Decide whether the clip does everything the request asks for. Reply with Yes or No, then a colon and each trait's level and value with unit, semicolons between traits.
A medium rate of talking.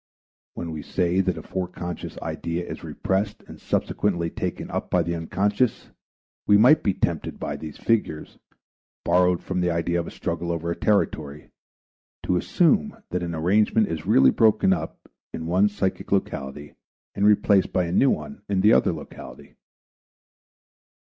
Yes: average, 160 wpm